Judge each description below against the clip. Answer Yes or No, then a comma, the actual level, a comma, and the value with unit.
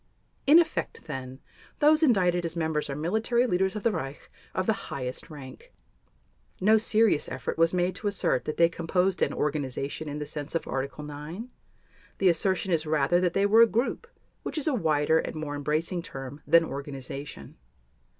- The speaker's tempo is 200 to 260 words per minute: No, average, 180 wpm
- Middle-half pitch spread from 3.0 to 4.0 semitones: No, wide, 5.5 semitones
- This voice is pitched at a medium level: Yes, medium, 165 Hz